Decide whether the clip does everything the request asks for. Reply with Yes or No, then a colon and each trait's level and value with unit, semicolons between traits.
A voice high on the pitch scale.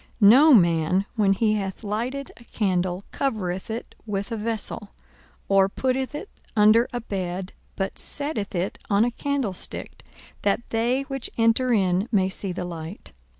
Yes: high, 210 Hz